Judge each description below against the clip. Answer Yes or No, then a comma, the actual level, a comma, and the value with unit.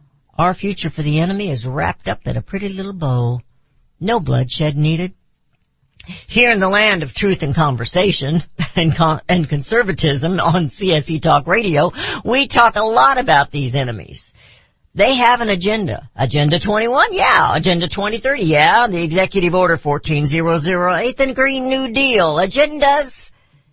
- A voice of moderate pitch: Yes, medium, 175 Hz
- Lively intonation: Yes, wide, 5.9 semitones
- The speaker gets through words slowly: No, average, 145 wpm